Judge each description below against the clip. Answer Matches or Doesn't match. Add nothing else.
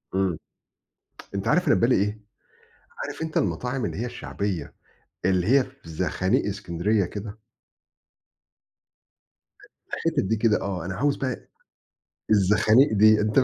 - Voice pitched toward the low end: Matches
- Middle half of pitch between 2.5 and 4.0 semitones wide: Doesn't match